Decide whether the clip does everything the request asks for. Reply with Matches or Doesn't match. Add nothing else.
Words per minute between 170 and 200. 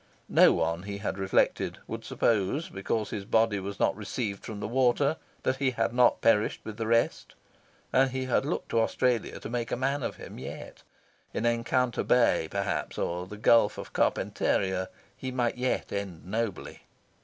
Matches